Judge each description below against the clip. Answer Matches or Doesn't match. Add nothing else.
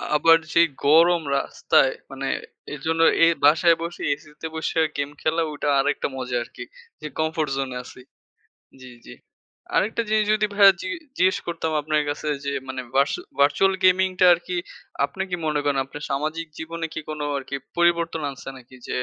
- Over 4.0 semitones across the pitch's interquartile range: Doesn't match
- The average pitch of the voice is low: Doesn't match